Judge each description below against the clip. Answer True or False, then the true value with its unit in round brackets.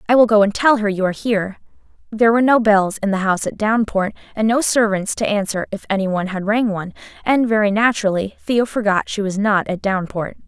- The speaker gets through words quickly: True (225 wpm)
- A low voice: False (210 Hz)